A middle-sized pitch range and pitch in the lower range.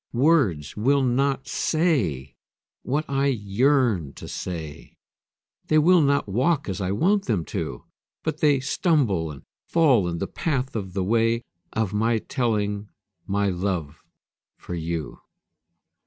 No: wide, 7.1 semitones; low, 115 Hz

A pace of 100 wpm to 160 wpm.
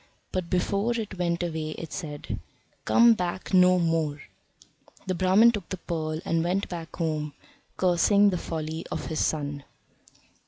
Yes: average, 150 wpm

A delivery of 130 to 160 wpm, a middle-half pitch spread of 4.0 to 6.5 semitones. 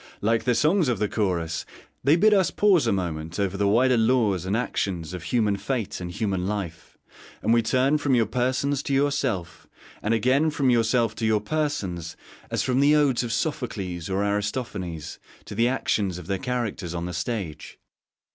No: average, 185 wpm; wide, 5.5 semitones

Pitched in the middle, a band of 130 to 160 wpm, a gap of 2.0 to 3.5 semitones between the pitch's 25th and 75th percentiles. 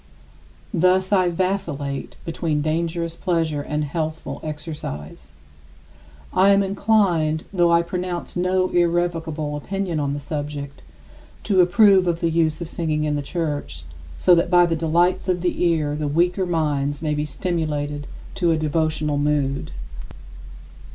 Yes: medium, 165 Hz; average, 140 wpm; average, 2.9 semitones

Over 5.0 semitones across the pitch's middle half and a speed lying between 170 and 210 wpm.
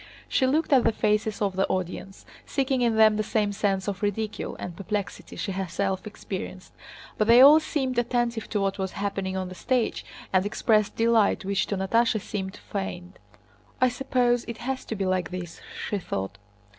No: average, 3.5 semitones; average, 180 wpm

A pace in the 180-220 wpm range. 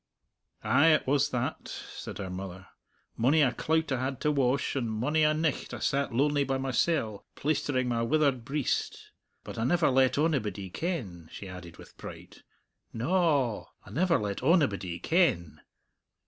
No: average, 165 wpm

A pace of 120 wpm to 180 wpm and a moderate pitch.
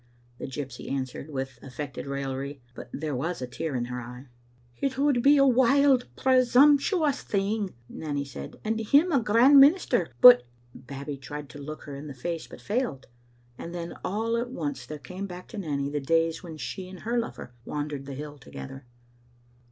No: average, 190 wpm; medium, 155 Hz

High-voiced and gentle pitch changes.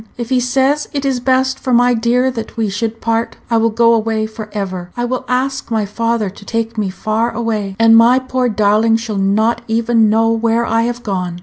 Yes: high, 230 Hz; narrow, 2.0 semitones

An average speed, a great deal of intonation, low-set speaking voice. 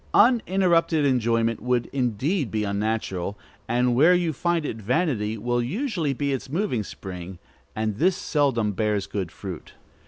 Yes: average, 145 wpm; wide, 7.2 semitones; low, 120 Hz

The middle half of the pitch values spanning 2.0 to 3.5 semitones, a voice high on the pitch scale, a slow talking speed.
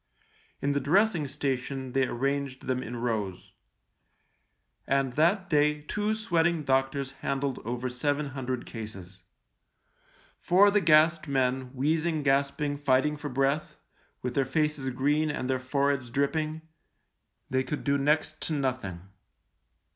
No: average, 2.8 semitones; medium, 140 Hz; slow, 130 wpm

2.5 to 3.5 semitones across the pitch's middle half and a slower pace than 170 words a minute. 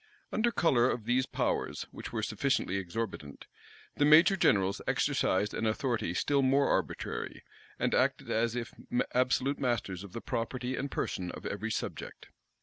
No: average, 4.8 semitones; average, 150 wpm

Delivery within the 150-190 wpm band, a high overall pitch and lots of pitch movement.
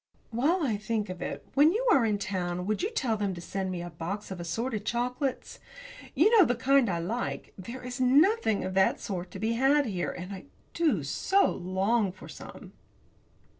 No: average, 200 wpm; high, 220 Hz; wide, 6.1 semitones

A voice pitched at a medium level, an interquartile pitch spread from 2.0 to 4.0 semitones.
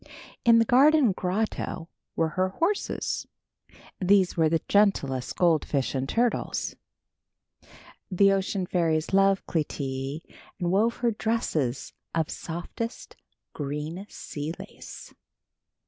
No: medium, 180 Hz; average, 5.1 semitones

